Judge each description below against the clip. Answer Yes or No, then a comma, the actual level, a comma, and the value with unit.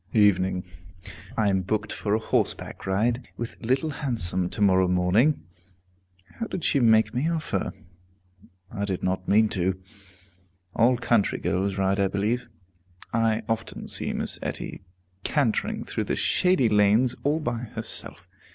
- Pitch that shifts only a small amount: No, average, 4.2 semitones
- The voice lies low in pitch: Yes, low, 110 Hz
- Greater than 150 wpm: No, average, 140 wpm